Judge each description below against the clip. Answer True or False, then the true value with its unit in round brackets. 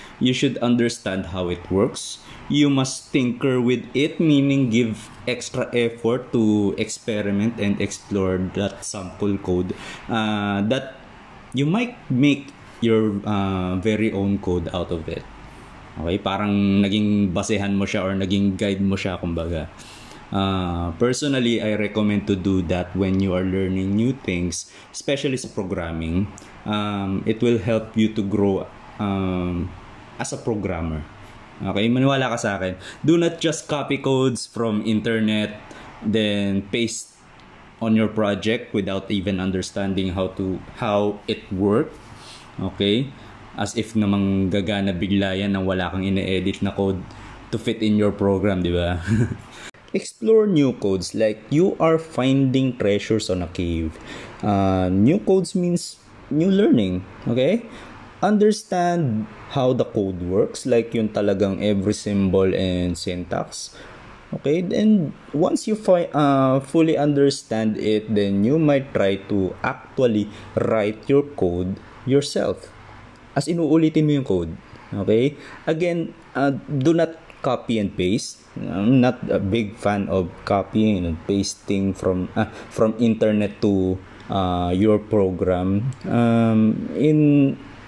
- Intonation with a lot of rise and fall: False (4.4 semitones)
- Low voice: True (105 Hz)